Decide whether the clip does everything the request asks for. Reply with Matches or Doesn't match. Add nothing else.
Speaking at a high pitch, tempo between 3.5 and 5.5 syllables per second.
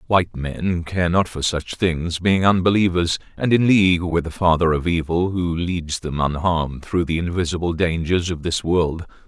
Doesn't match